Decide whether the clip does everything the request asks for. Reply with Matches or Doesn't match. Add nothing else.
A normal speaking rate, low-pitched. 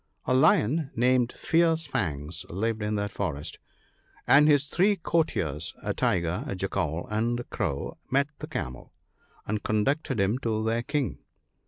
Matches